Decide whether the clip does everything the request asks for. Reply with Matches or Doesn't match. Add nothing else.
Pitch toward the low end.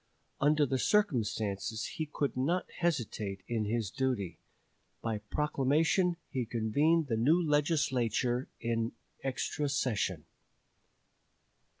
Matches